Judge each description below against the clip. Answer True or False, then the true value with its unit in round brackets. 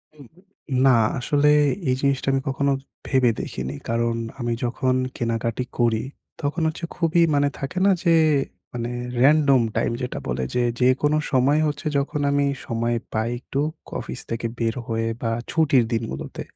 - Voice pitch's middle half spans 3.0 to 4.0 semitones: True (3.4 semitones)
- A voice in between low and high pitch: False (130 Hz)